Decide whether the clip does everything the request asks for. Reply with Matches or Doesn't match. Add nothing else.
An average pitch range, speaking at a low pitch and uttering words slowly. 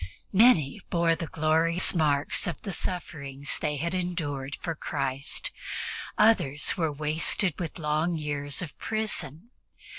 Doesn't match